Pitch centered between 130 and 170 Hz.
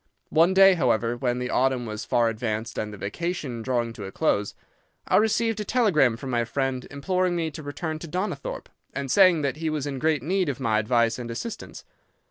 Yes: low, 135 Hz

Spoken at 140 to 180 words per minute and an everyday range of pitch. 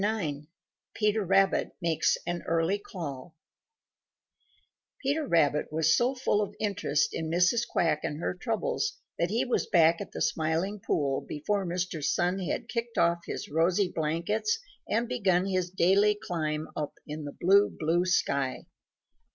Yes: average, 150 wpm; average, 4.4 semitones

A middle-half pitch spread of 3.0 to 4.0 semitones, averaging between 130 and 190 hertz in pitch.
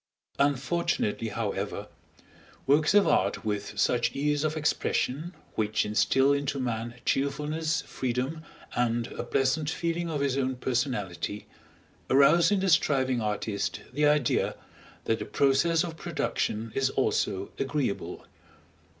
No: average, 4.8 semitones; low, 135 Hz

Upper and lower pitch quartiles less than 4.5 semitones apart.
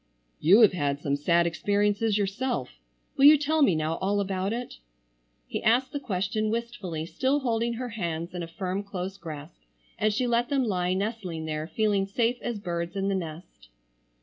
No: average, 5.3 semitones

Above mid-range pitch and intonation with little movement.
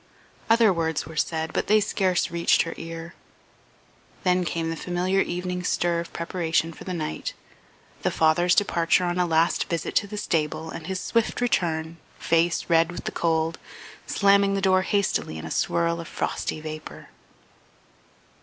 No: medium, 170 Hz; narrow, 2.3 semitones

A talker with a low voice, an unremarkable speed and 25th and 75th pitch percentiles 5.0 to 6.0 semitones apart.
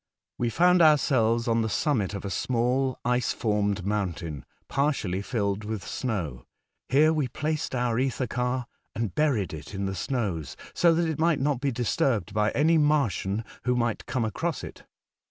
Yes: low, 120 Hz; average, 170 wpm; wide, 5.4 semitones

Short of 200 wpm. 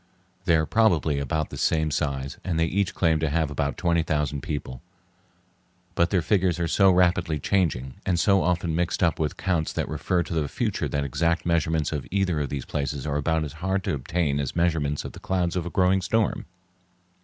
No: fast, 205 wpm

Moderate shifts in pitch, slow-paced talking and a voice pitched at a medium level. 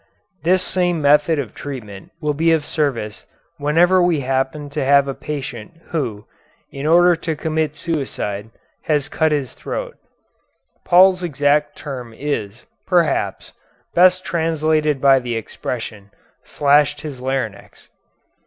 Yes: average, 3.5 semitones; slow, 125 wpm; medium, 145 Hz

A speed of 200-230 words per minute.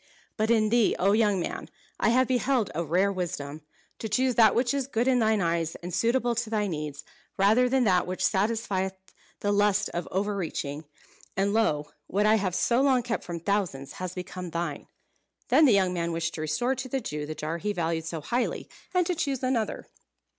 Yes: fast, 205 wpm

